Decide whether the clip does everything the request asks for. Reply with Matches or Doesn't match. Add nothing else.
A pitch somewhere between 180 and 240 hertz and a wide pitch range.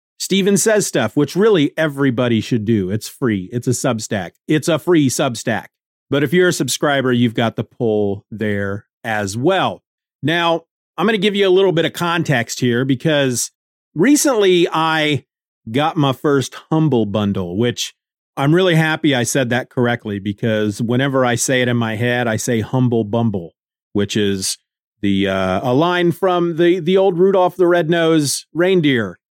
Doesn't match